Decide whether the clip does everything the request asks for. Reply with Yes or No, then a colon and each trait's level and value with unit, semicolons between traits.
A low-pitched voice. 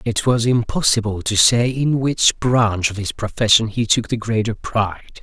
Yes: low, 115 Hz